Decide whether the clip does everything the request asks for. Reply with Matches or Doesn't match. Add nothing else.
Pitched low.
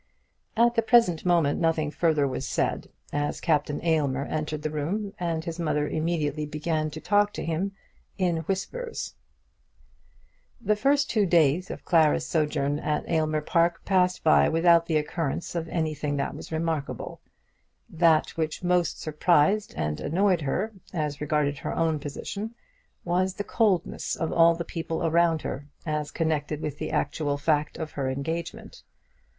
Doesn't match